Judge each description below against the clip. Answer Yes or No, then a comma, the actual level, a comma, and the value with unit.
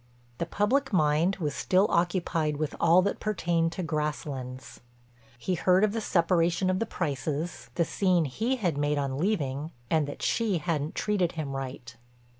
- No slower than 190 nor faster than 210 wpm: No, average, 165 wpm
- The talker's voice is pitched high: No, medium, 165 Hz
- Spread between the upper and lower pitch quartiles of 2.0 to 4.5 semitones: Yes, average, 4.0 semitones